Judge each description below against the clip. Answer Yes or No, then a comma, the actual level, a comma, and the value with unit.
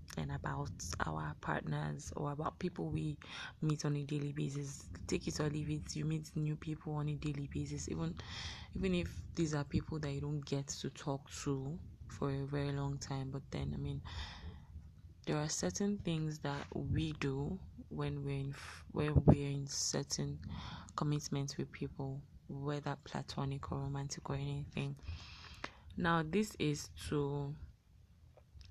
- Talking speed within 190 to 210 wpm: No, average, 155 wpm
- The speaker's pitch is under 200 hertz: Yes, medium, 140 Hz